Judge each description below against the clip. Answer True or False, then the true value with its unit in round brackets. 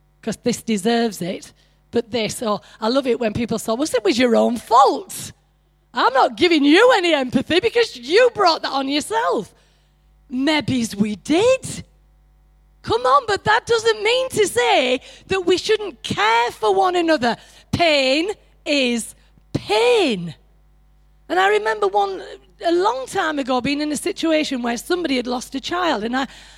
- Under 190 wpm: True (165 wpm)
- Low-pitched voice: False (305 Hz)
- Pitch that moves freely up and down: True (8.8 semitones)